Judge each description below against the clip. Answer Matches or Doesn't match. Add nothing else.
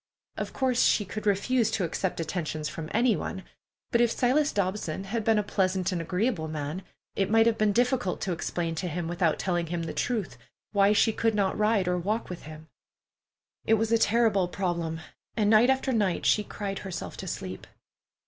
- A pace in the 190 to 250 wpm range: Matches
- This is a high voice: Matches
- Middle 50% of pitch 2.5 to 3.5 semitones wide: Doesn't match